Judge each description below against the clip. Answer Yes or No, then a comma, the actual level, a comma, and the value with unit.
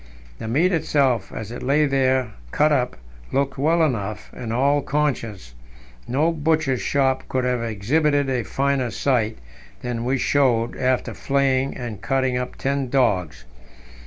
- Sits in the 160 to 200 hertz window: No, low, 130 Hz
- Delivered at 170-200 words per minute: No, average, 145 wpm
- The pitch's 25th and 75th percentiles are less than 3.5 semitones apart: Yes, average, 2.9 semitones